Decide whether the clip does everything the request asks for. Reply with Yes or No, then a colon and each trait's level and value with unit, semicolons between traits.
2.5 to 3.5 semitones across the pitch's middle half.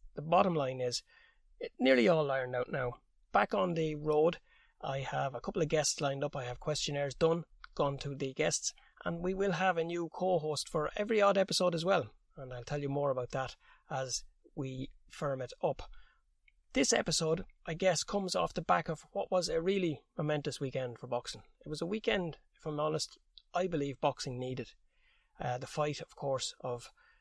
No: average, 4.6 semitones